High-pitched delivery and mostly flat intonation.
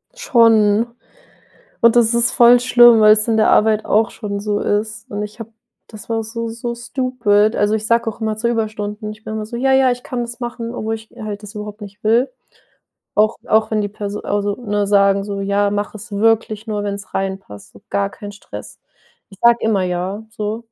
Yes: high, 215 Hz; narrow, 2.0 semitones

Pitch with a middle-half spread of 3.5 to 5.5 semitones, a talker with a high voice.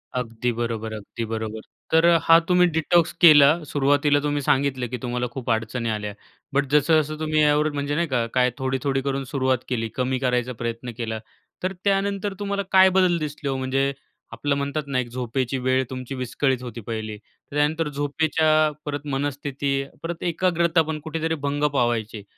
No: average, 3.8 semitones; medium, 140 Hz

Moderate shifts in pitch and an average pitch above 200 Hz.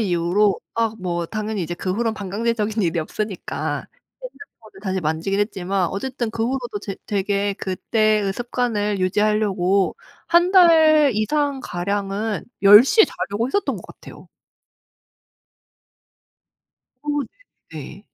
Yes: average, 3.3 semitones; high, 210 Hz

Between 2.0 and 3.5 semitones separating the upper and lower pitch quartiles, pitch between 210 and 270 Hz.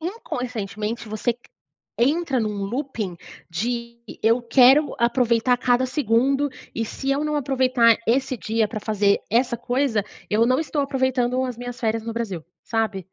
Yes: average, 2.8 semitones; high, 240 Hz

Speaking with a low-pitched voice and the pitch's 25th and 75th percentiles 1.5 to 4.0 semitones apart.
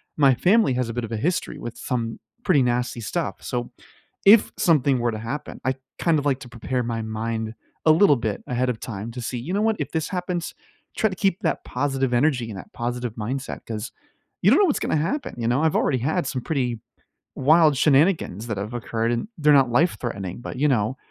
No: low, 125 Hz; average, 4.6 semitones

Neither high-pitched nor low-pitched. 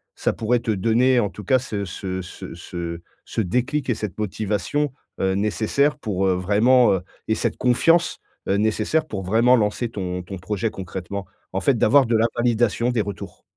No: low, 110 Hz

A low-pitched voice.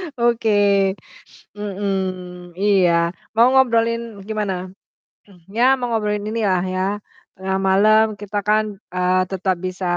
No: high, 200 Hz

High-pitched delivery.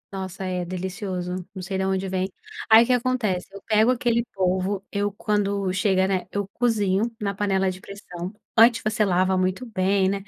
Yes: high, 195 Hz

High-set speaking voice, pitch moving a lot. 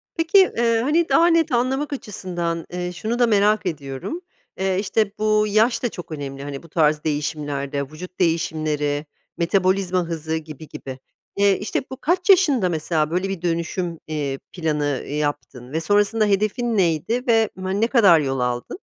No: medium, 180 Hz; wide, 6.3 semitones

